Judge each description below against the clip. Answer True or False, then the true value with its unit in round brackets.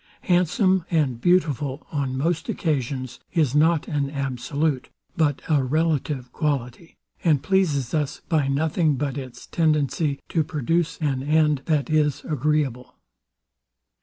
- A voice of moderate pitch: True (150 Hz)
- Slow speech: True (125 wpm)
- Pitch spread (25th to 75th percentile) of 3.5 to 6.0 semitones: False (2.9 semitones)